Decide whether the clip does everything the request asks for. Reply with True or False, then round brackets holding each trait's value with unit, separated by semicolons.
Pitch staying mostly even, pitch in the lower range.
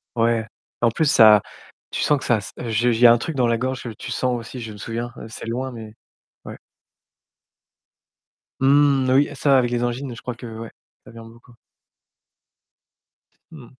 True (2.3 semitones; 120 Hz)